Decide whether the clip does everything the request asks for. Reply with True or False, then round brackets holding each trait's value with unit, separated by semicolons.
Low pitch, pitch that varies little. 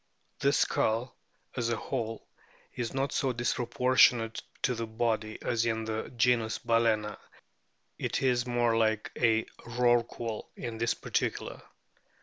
True (115 Hz; 1.5 semitones)